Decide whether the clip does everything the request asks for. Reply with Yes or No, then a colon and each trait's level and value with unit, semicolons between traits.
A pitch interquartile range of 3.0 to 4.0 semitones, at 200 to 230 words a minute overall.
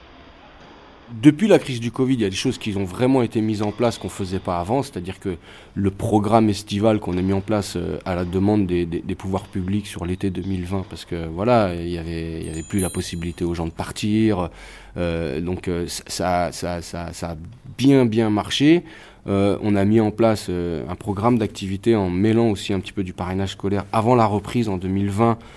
Yes: average, 3.7 semitones; average, 215 wpm